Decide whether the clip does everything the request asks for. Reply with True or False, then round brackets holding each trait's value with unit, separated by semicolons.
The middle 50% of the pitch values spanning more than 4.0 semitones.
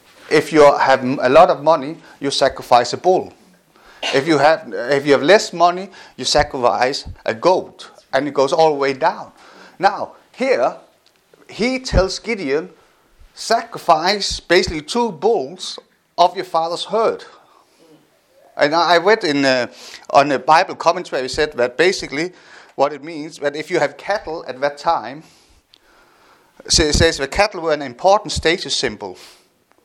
True (4.7 semitones)